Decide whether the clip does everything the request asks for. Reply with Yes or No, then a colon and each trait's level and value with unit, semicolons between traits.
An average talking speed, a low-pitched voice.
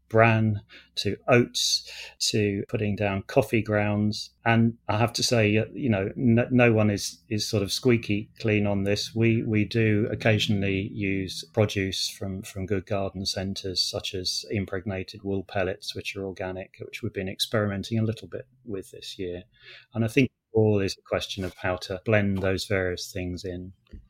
Yes: average, 175 wpm; low, 105 Hz